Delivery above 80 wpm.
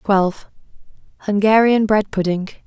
No: slow, 70 wpm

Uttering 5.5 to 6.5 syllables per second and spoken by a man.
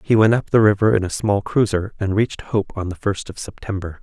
Yes: 5.7 syllables/s; male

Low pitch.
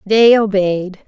No: high, 200 Hz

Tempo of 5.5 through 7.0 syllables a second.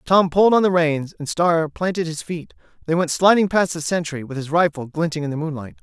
Yes: 5.7 syllables/s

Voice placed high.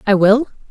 Yes: high, 220 Hz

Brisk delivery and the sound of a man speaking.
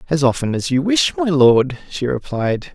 No: average, 195 wpm; male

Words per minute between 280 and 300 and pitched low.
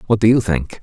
Yes: fast, 290 wpm; low, 100 Hz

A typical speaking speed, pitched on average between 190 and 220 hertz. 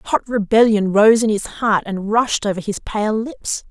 Yes: average, 195 wpm; high, 215 Hz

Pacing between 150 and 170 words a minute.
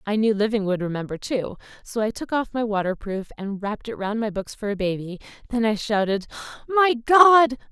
No: average, 200 wpm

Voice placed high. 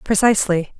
Yes: high, 195 Hz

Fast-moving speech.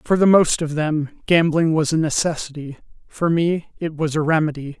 No: average, 190 wpm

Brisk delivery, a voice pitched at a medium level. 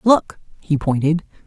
No: slow, 125 wpm; medium, 165 Hz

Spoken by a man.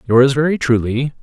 Yes: male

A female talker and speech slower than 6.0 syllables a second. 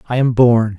No: male; 4.9 syllables/s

